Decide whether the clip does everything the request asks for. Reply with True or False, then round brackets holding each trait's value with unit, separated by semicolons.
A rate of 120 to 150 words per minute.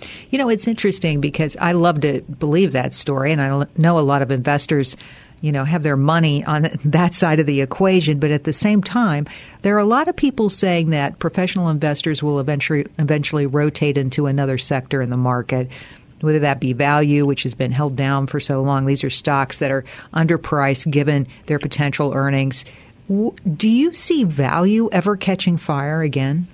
False (190 wpm)